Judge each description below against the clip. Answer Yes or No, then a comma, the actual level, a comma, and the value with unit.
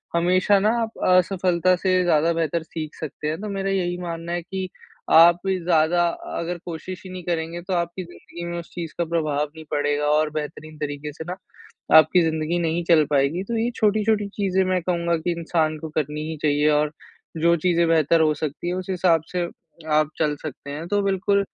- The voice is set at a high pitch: No, medium, 170 Hz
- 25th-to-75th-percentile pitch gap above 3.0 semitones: No, average, 2.7 semitones